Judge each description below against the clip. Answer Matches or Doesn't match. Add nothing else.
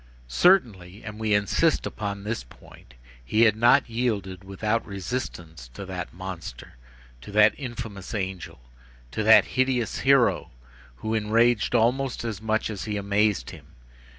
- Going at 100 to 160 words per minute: Matches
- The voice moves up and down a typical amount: Matches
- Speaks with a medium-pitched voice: Doesn't match